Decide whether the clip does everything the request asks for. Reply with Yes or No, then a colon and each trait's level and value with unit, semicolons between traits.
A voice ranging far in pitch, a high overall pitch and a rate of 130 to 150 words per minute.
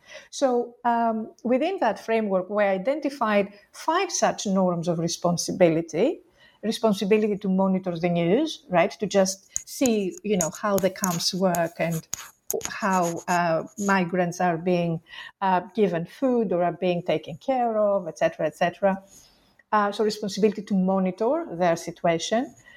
No: average, 3.8 semitones; high, 195 Hz; average, 140 wpm